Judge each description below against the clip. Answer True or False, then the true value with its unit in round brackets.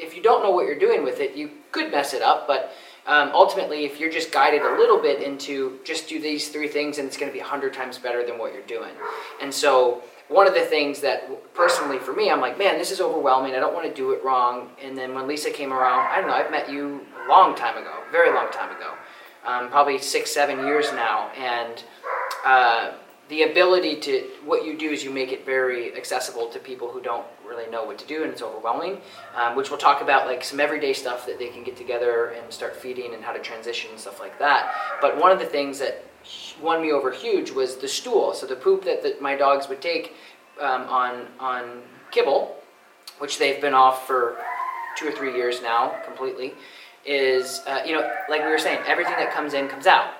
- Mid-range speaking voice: True (155 Hz)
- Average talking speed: False (230 wpm)